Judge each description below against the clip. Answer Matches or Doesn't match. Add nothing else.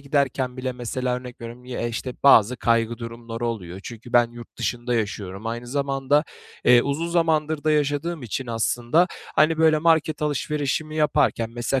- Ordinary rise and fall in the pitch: Matches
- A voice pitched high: Doesn't match